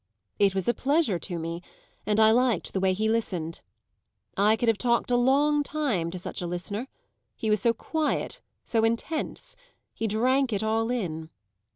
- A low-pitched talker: No, high, 220 Hz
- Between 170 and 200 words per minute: Yes, average, 180 wpm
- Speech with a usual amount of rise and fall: Yes, average, 4.6 semitones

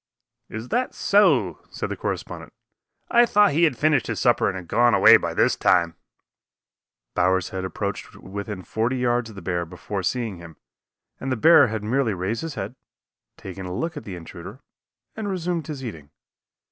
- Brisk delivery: No, average, 185 wpm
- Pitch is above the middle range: No, low, 110 Hz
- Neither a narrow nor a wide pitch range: No, wide, 7.4 semitones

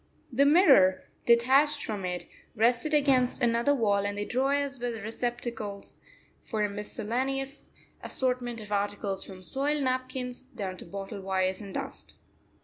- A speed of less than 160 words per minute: Yes, average, 140 wpm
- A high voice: Yes, high, 235 Hz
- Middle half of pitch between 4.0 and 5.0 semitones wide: Yes, average, 4.6 semitones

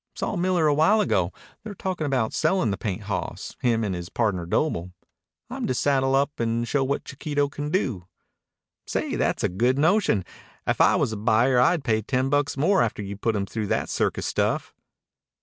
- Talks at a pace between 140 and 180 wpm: No, average, 195 wpm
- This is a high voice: No, low, 130 Hz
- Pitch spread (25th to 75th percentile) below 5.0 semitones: No, wide, 5.6 semitones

